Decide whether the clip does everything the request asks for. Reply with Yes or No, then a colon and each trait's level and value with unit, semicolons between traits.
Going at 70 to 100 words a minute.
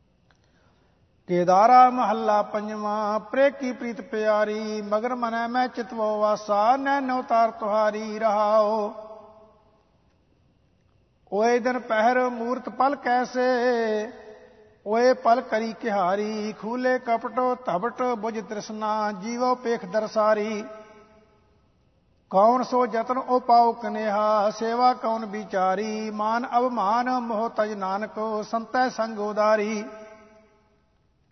Yes: slow, 95 wpm